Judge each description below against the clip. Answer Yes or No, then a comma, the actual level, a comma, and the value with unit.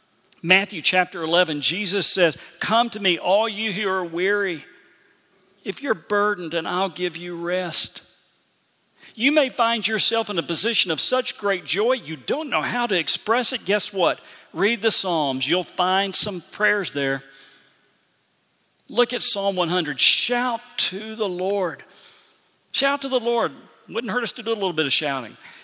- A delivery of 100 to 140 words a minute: No, average, 165 wpm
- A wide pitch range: No, average, 4.5 semitones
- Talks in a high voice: Yes, high, 195 Hz